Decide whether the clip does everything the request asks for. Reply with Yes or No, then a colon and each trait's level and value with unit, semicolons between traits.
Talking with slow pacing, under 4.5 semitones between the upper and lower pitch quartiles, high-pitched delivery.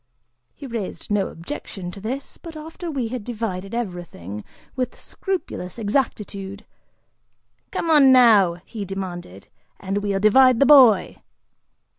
No: slow, 125 wpm; average, 5.3 semitones; high, 215 Hz